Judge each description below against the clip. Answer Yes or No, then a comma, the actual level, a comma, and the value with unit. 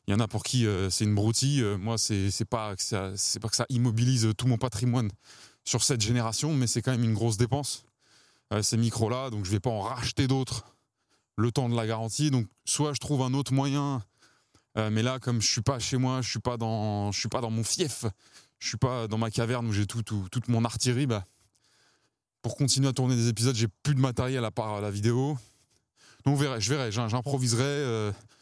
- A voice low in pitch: Yes, low, 120 Hz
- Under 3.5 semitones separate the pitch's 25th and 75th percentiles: Yes, average, 3.0 semitones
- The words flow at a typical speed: No, fast, 225 wpm